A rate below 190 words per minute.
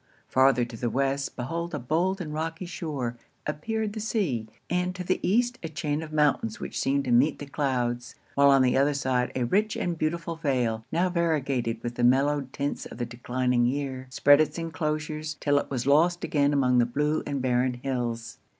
No: average, 195 wpm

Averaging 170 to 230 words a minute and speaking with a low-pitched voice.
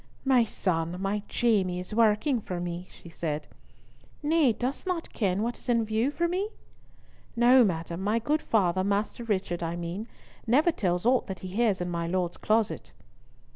No: average, 175 wpm; high, 210 Hz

